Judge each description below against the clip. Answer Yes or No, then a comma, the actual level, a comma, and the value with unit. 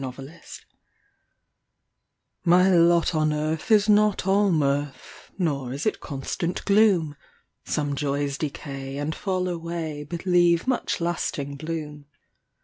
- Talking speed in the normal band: No, slow, 125 wpm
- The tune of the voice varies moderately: Yes, average, 3.9 semitones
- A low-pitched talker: No, medium, 160 Hz